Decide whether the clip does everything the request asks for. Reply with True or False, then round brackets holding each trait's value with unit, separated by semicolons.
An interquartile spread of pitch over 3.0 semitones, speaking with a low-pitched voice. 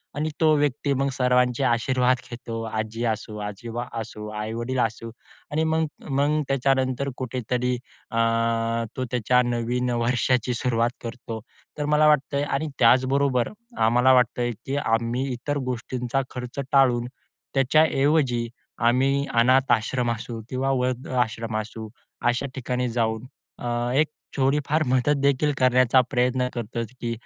False (2.4 semitones; 125 Hz)